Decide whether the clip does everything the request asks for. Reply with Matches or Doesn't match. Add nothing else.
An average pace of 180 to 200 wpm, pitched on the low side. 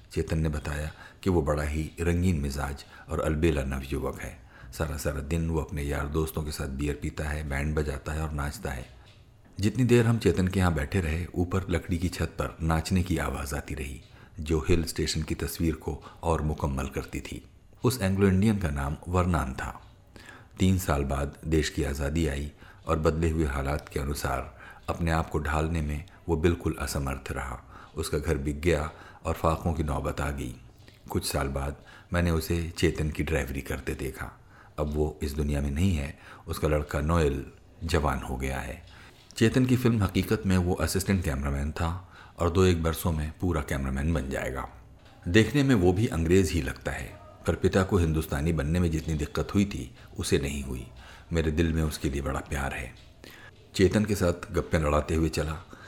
Matches